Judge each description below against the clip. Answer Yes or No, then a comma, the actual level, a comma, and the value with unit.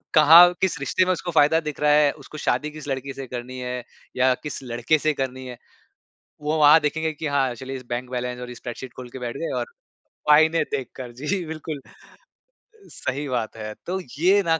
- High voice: No, medium, 140 Hz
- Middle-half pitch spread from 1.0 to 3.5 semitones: No, average, 3.9 semitones